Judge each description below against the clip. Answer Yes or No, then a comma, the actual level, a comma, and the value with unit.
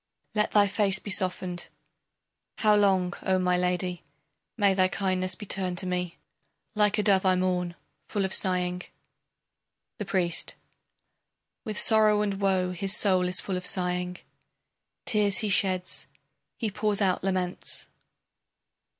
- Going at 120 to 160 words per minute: Yes, average, 140 wpm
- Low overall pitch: No, high, 190 Hz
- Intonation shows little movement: Yes, narrow, 2.0 semitones